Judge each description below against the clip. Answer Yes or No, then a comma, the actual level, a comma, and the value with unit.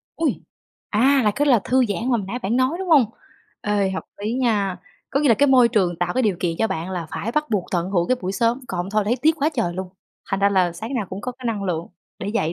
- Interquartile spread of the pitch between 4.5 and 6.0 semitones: Yes, average, 5.2 semitones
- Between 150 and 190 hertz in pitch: No, high, 215 Hz